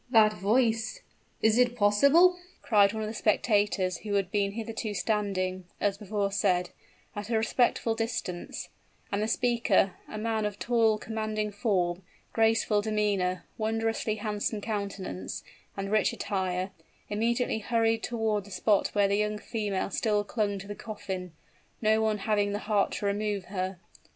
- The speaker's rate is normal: Yes, average, 150 wpm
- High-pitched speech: Yes, high, 210 Hz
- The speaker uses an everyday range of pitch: No, narrow, 2.0 semitones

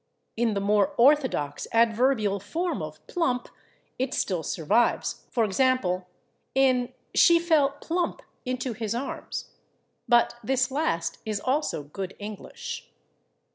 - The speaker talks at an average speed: No, slow, 120 wpm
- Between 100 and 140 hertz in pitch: No, high, 240 Hz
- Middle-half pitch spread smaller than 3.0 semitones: No, average, 5.0 semitones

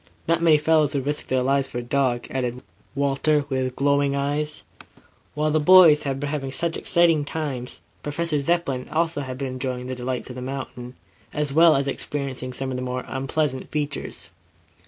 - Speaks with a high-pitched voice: No, medium, 140 Hz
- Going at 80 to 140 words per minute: No, average, 180 wpm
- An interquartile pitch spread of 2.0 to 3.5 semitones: Yes, average, 2.7 semitones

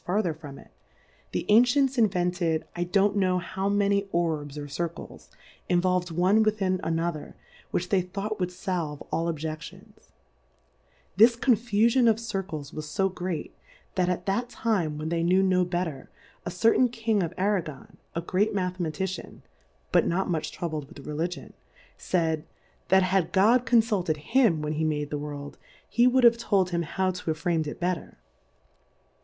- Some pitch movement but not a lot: Yes, average, 3.9 semitones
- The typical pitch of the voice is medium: Yes, medium, 180 Hz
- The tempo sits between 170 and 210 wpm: No, average, 160 wpm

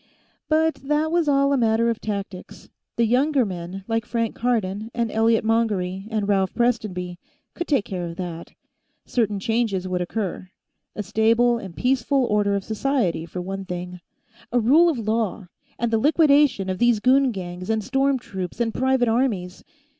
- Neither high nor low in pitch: No, high, 225 Hz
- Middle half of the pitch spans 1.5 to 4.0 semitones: No, average, 4.6 semitones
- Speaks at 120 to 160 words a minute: No, average, 170 wpm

